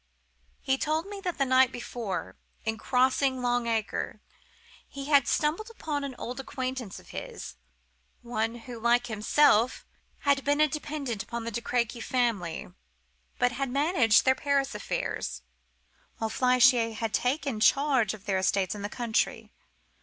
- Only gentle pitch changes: No, average, 3.7 semitones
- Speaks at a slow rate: No, average, 150 wpm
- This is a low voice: No, high, 245 Hz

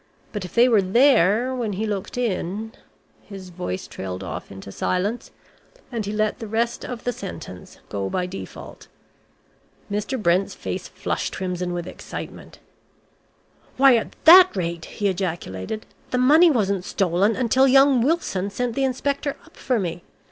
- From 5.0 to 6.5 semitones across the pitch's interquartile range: Yes, wide, 5.5 semitones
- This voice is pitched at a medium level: No, high, 210 Hz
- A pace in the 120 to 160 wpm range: Yes, average, 155 wpm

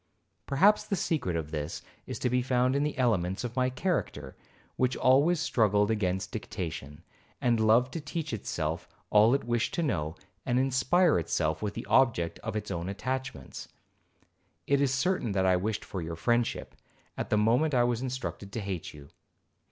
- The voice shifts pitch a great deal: Yes, wide, 6.0 semitones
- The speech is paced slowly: No, average, 175 wpm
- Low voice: Yes, low, 115 Hz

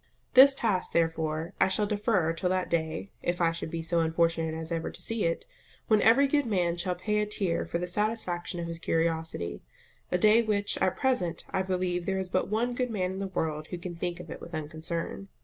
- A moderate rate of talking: No, fast, 220 wpm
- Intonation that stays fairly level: No, average, 3.9 semitones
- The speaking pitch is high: No, medium, 180 Hz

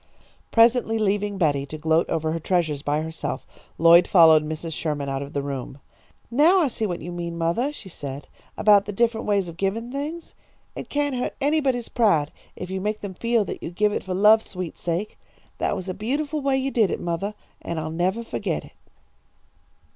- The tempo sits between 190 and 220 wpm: Yes, average, 200 wpm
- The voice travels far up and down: Yes, wide, 6.0 semitones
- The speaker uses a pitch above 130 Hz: Yes, high, 190 Hz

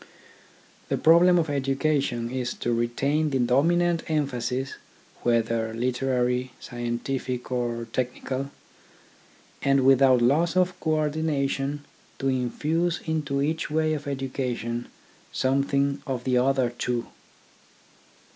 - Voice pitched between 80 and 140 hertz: Yes, low, 135 Hz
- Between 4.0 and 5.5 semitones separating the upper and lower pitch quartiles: No, average, 3.3 semitones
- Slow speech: Yes, slow, 110 wpm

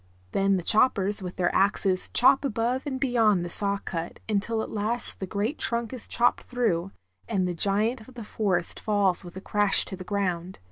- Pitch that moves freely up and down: No, average, 3.7 semitones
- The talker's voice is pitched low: No, high, 205 Hz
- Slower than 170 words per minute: No, average, 195 wpm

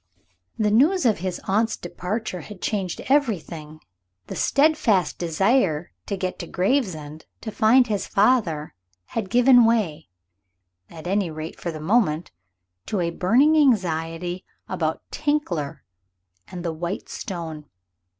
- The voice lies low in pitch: No, medium, 185 Hz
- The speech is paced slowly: Yes, slow, 130 wpm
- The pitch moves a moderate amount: No, wide, 5.8 semitones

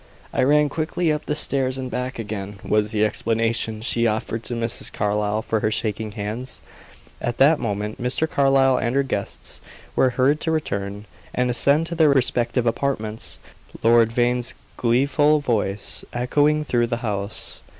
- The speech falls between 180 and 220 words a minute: No, average, 160 wpm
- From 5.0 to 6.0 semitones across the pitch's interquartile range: No, average, 4.1 semitones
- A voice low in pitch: Yes, low, 120 Hz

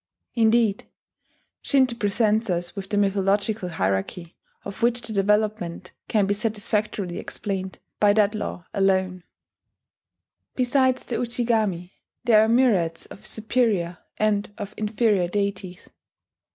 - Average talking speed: No, slow, 115 wpm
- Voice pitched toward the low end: No, high, 205 Hz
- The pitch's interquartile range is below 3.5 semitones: Yes, average, 2.9 semitones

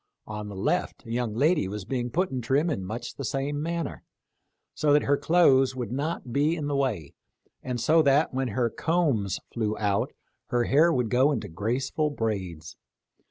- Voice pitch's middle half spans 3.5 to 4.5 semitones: No, average, 5.1 semitones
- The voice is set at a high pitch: No, low, 130 Hz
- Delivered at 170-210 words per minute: Yes, average, 185 wpm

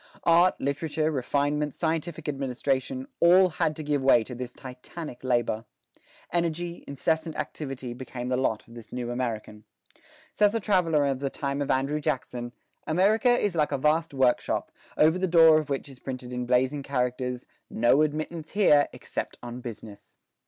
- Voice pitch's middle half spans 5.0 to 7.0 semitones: No, average, 4.3 semitones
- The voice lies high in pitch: No, medium, 140 Hz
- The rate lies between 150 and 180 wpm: Yes, average, 160 wpm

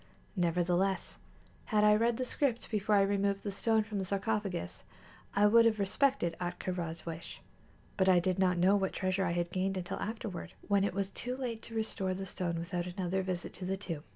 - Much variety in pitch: No, average, 2.8 semitones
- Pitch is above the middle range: Yes, high, 195 Hz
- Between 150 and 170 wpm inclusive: No, fast, 205 wpm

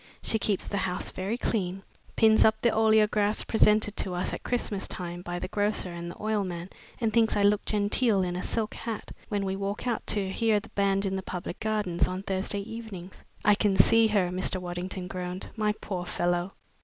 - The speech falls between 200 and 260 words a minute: Yes, fast, 205 wpm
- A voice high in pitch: Yes, high, 200 Hz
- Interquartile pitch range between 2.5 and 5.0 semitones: Yes, average, 2.9 semitones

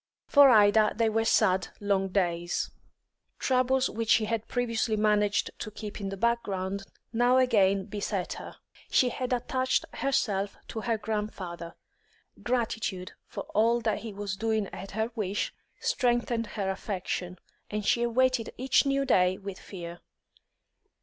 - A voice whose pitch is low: No, high, 215 Hz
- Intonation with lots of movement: No, average, 3.4 semitones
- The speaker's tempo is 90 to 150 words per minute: Yes, average, 145 wpm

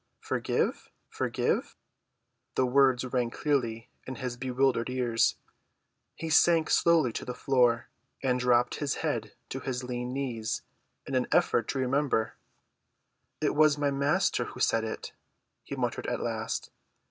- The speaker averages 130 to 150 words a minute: Yes, slow, 135 wpm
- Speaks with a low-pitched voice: Yes, low, 125 Hz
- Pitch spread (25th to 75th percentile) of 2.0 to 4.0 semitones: Yes, narrow, 2.4 semitones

